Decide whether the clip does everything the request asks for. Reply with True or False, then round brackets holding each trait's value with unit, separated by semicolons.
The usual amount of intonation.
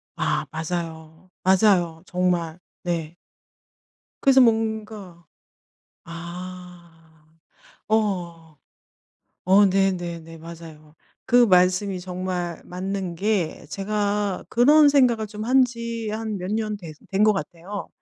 True (3.9 semitones)